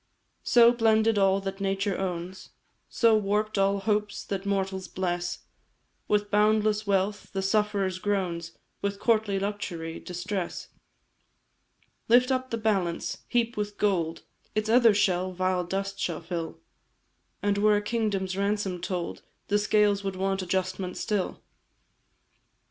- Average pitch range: No, narrow, 2.1 semitones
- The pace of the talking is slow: Yes, slow, 130 wpm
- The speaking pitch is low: No, high, 200 Hz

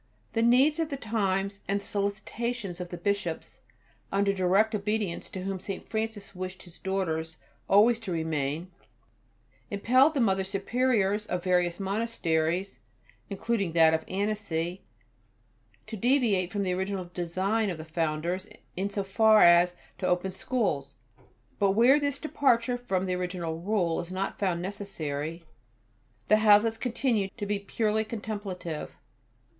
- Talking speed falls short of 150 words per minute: Yes, average, 140 wpm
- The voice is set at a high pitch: Yes, high, 195 Hz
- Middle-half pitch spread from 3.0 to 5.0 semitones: Yes, average, 3.6 semitones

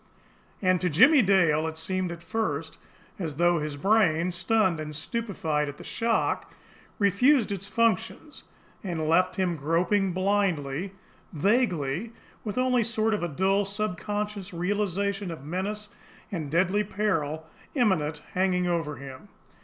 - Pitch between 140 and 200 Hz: Yes, medium, 185 Hz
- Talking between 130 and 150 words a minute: Yes, average, 140 wpm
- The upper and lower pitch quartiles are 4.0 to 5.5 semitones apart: Yes, average, 4.5 semitones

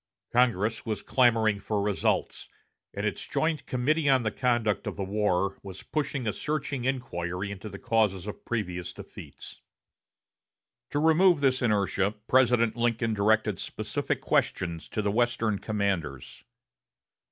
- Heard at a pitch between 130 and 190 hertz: No, low, 110 Hz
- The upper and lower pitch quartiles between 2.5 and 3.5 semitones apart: No, average, 4.0 semitones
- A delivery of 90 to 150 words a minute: Yes, slow, 135 wpm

